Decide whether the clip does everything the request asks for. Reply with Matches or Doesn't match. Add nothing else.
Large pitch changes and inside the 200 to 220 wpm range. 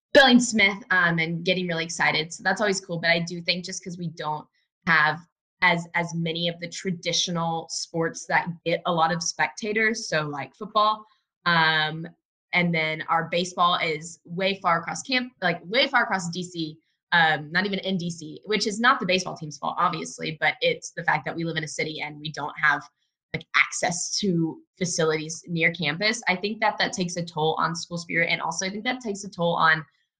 Doesn't match